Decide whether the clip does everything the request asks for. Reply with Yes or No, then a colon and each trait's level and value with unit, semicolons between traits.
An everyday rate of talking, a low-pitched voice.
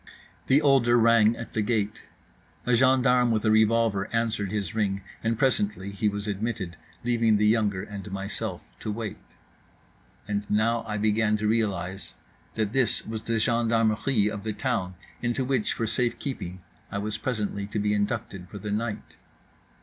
Yes: average, 165 wpm; low, 110 Hz